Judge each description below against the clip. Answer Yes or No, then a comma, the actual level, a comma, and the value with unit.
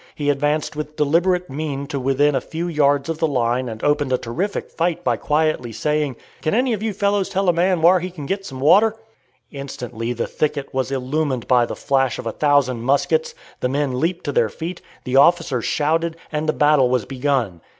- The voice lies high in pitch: No, medium, 145 Hz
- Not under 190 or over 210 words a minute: Yes, average, 200 wpm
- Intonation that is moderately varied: Yes, average, 4.2 semitones